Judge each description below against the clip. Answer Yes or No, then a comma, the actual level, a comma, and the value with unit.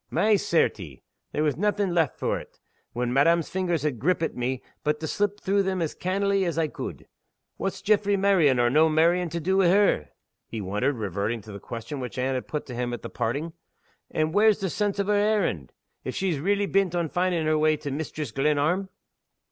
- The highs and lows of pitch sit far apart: Yes, wide, 6.4 semitones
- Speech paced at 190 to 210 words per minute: Yes, average, 200 wpm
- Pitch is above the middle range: No, medium, 160 Hz